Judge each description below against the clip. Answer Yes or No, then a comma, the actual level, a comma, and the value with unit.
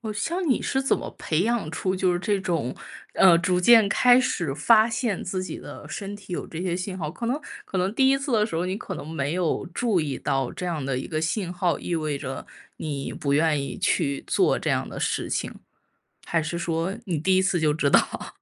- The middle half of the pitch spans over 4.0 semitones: Yes, average, 4.9 semitones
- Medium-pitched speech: Yes, medium, 180 Hz